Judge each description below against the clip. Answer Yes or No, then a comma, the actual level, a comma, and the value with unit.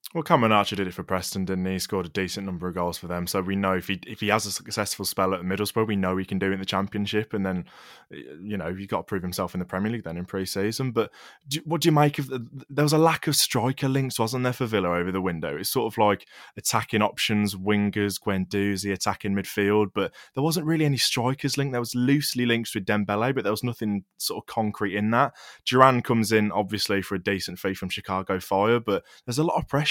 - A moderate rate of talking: No, fast, 260 wpm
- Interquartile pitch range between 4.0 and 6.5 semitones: Yes, average, 4.5 semitones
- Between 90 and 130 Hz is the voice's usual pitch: Yes, low, 105 Hz